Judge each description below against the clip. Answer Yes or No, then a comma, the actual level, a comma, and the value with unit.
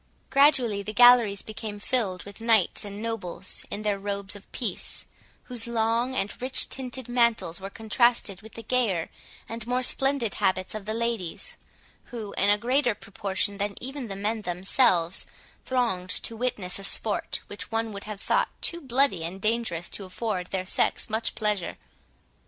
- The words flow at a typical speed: Yes, average, 165 wpm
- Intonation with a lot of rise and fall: No, average, 3.3 semitones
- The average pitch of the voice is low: No, high, 215 Hz